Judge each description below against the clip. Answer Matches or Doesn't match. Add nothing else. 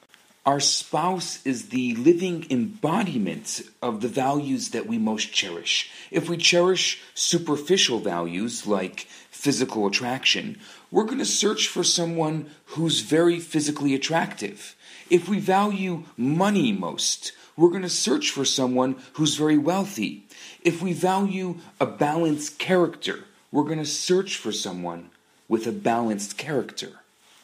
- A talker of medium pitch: Matches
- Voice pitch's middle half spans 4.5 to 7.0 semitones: Matches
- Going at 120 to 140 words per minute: Matches